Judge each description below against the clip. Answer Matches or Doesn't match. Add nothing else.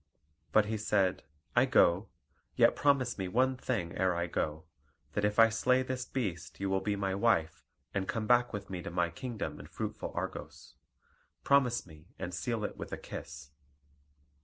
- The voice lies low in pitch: Matches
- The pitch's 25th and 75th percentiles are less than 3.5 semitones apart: Doesn't match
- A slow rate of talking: Doesn't match